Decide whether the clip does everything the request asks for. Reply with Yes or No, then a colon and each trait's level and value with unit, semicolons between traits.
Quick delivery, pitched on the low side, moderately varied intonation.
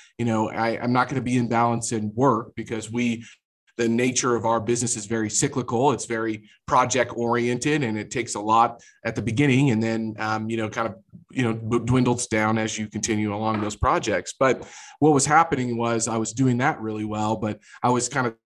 No: fast, 220 wpm; low, 115 Hz; narrow, 2.0 semitones